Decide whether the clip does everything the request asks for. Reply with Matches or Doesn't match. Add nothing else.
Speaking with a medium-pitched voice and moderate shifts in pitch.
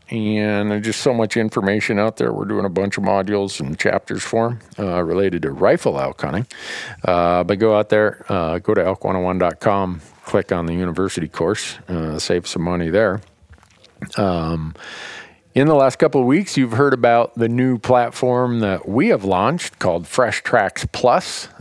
Doesn't match